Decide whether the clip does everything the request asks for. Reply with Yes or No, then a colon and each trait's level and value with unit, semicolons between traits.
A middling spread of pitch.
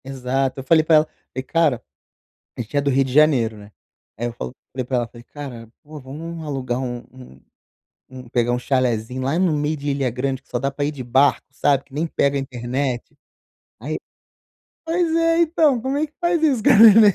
Yes: average, 4.1 semitones